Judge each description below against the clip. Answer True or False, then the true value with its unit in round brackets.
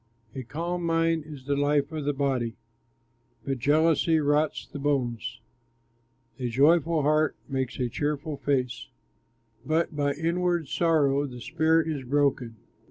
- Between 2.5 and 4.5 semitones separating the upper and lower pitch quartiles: True (3.1 semitones)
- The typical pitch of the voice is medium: True (145 Hz)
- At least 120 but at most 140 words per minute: True (135 wpm)